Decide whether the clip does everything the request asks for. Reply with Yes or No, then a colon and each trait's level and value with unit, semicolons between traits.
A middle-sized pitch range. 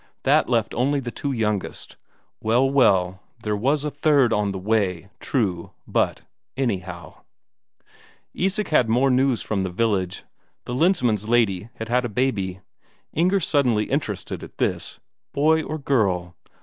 No: wide, 5.7 semitones